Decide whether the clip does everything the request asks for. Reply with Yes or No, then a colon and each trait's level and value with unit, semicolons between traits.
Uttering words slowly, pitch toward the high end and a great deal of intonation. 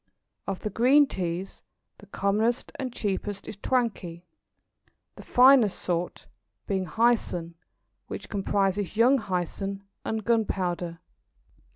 No: slow, 105 wpm; high, 200 Hz; average, 4.0 semitones